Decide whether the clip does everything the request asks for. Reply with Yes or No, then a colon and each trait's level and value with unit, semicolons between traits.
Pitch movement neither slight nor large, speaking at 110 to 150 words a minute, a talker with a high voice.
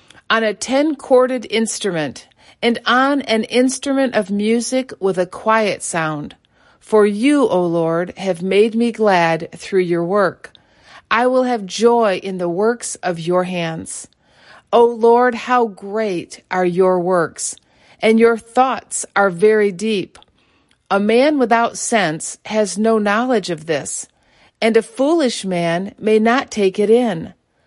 Yes: average, 4.1 semitones; average, 145 wpm; high, 220 Hz